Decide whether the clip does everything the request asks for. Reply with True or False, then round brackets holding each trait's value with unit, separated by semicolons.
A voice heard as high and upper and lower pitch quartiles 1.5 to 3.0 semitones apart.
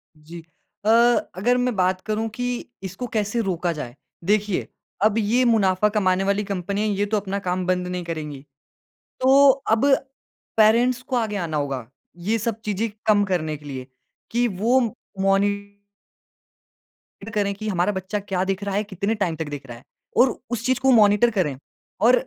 False (200 Hz; 3.7 semitones)